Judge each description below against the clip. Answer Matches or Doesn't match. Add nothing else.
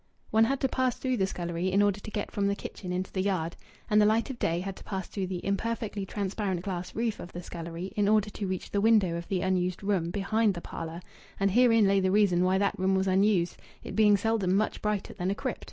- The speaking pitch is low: Doesn't match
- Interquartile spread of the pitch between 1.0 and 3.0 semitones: Matches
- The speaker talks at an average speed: Doesn't match